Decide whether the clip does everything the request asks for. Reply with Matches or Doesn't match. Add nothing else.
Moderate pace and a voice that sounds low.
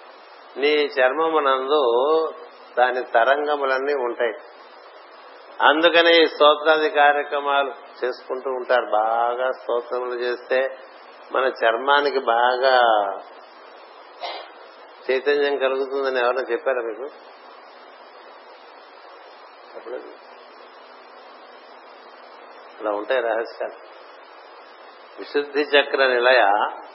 Doesn't match